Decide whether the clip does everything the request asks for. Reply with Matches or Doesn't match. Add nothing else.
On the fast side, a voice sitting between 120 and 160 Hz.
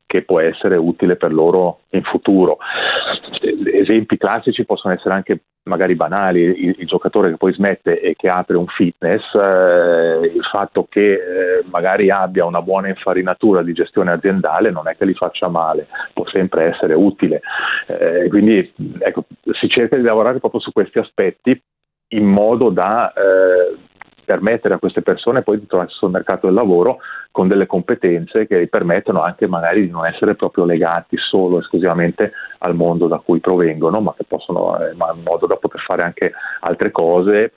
Doesn't match